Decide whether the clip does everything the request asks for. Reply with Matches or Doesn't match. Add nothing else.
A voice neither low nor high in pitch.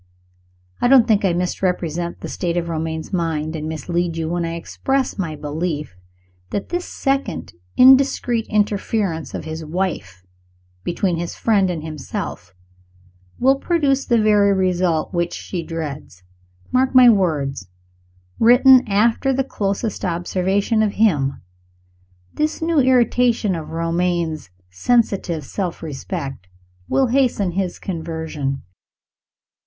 Matches